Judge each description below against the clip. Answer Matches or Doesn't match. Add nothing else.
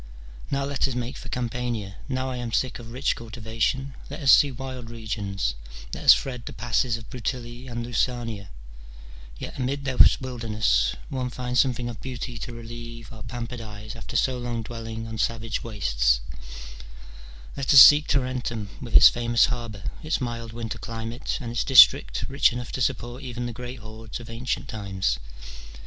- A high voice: Doesn't match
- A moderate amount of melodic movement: Doesn't match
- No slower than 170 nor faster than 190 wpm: Matches